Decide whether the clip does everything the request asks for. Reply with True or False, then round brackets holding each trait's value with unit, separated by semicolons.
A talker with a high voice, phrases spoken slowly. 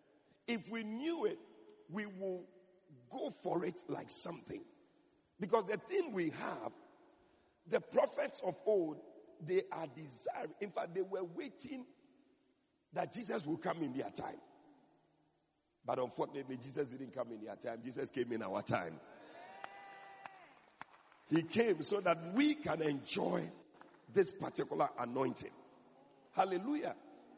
True (230 Hz; 130 wpm)